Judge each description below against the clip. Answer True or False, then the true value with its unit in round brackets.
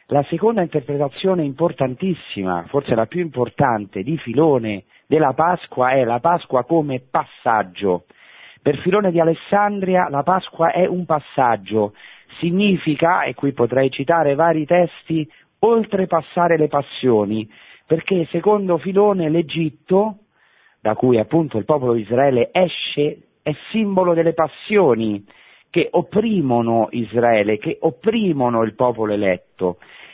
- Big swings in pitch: True (6.4 semitones)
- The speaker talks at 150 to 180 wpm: False (120 wpm)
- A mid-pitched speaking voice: True (155 Hz)